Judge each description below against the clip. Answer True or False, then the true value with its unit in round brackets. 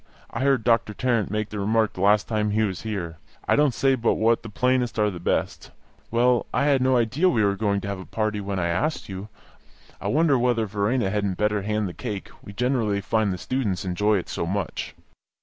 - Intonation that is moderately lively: True (3.4 semitones)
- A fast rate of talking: True (220 wpm)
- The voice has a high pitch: False (110 Hz)